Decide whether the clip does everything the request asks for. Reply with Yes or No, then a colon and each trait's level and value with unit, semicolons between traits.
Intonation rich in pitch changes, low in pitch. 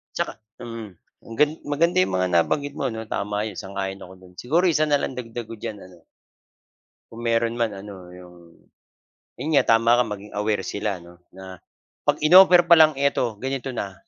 Yes: wide, 5.9 semitones; low, 115 Hz